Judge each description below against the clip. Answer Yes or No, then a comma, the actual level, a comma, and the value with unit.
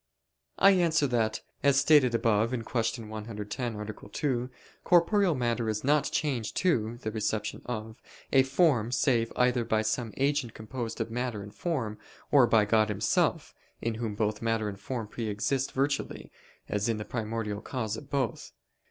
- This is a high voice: No, low, 115 Hz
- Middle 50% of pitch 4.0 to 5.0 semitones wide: No, average, 3.5 semitones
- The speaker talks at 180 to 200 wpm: No, average, 160 wpm